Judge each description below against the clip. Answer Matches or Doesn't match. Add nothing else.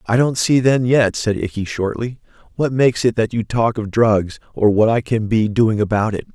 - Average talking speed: Doesn't match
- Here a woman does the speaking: Doesn't match